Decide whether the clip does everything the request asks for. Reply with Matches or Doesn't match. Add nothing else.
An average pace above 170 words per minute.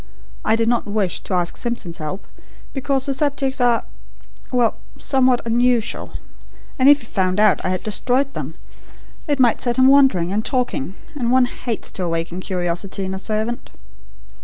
Doesn't match